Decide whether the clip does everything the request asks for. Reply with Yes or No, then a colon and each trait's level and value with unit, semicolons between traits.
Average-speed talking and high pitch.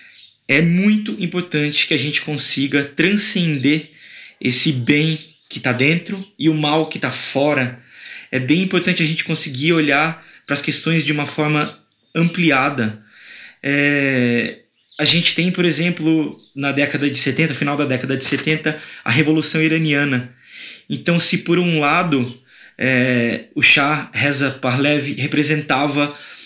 No: average, 135 wpm; medium, 150 Hz